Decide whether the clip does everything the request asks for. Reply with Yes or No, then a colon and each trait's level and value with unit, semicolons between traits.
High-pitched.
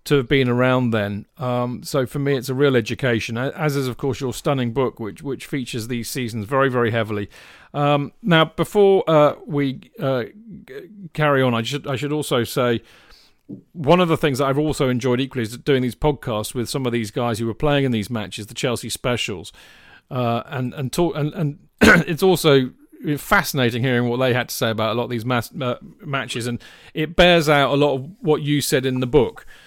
No: low, 135 Hz